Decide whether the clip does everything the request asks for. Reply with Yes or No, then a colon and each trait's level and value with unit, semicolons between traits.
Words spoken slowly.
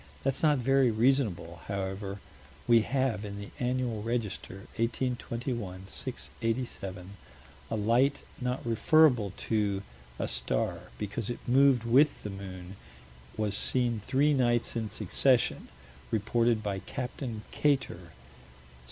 Yes: slow, 115 wpm